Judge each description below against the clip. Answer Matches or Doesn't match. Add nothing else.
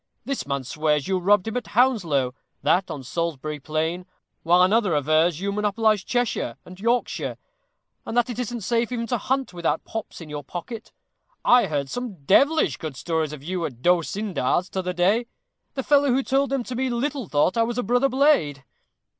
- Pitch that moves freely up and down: Matches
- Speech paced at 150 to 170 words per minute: Doesn't match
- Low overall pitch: Doesn't match